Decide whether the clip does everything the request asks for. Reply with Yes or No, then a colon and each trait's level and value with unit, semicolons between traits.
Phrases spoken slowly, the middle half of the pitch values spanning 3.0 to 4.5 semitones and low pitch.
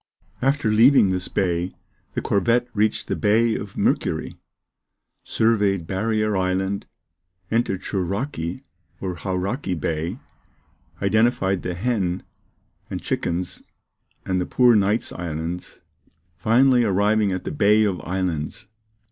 Yes: slow, 115 wpm; average, 3.6 semitones; low, 100 Hz